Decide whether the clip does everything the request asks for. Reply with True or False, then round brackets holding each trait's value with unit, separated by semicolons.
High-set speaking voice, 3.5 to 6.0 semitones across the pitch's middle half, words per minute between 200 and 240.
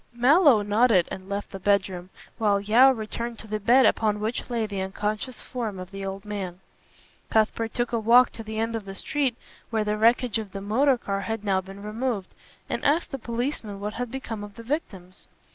False (215 Hz; 3.1 semitones; 205 wpm)